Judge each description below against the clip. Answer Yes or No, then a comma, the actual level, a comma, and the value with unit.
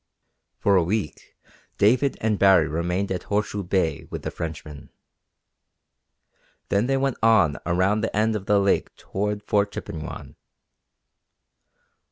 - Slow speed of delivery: Yes, slow, 130 wpm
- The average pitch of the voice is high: No, low, 100 Hz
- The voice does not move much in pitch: No, average, 3.4 semitones